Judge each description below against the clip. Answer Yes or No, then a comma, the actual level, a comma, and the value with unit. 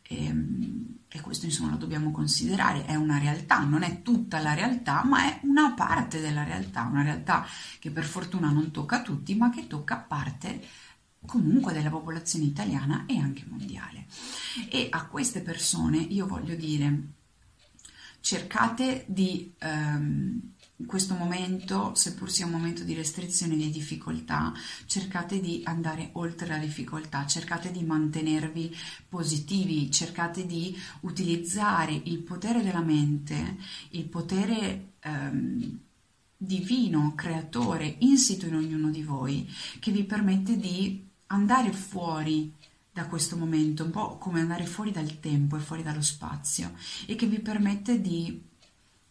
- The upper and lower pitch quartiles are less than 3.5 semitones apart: No, average, 4.3 semitones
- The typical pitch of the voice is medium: Yes, medium, 165 Hz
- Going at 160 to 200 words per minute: No, average, 140 wpm